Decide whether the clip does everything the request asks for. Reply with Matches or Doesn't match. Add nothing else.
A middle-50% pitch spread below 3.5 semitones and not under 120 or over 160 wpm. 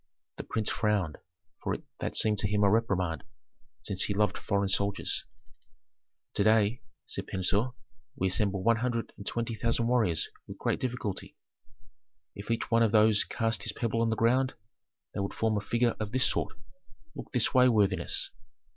Doesn't match